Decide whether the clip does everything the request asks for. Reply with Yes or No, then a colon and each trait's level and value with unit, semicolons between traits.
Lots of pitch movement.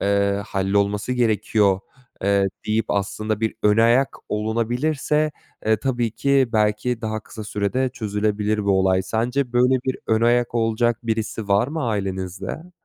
No: average, 3.1 semitones